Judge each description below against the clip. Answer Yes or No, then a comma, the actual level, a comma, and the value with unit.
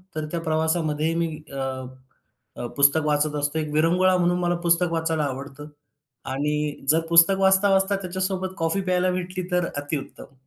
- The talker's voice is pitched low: No, medium, 165 Hz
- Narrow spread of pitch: No, average, 3.4 semitones